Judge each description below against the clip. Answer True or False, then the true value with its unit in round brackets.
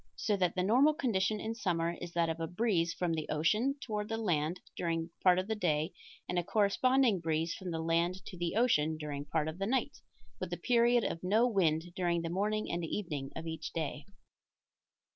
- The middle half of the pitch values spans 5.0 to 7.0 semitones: False (4.6 semitones)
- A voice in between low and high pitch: True (175 Hz)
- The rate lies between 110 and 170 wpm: False (205 wpm)